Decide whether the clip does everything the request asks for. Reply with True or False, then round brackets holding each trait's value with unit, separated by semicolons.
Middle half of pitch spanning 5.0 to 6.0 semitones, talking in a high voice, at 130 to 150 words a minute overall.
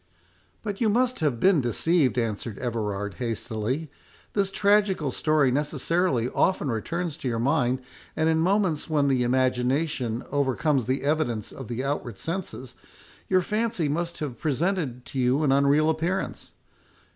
False (5.3 semitones; 145 Hz; 145 wpm)